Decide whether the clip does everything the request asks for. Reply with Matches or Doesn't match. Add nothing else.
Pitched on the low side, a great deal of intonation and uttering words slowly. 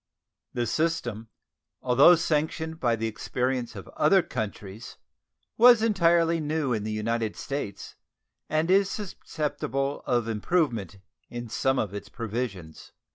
Matches